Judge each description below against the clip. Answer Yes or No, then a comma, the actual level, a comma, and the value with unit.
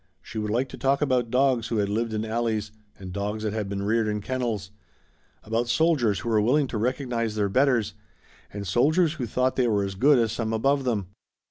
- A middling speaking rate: No, fast, 215 wpm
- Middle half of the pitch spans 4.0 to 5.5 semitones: No, average, 3.5 semitones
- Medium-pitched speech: No, low, 115 Hz